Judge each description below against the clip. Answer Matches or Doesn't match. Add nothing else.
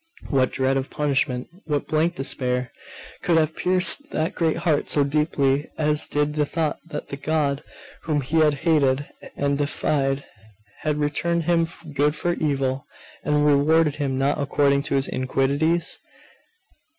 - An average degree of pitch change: Doesn't match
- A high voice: Doesn't match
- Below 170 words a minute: Matches